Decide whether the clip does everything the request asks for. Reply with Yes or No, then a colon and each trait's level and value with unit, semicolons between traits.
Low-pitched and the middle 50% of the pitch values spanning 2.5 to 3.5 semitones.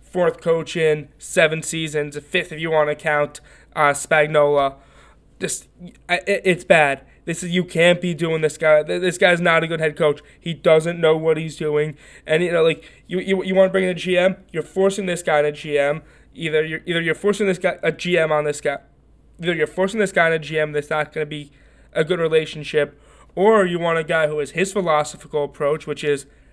No: medium, 160 Hz; average, 2.9 semitones